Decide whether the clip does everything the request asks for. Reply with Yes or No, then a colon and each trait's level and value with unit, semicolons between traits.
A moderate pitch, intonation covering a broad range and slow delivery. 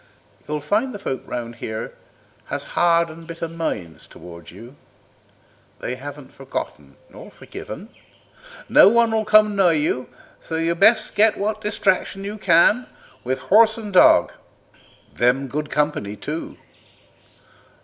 Yes: medium, 165 Hz; wide, 7.8 semitones; slow, 130 wpm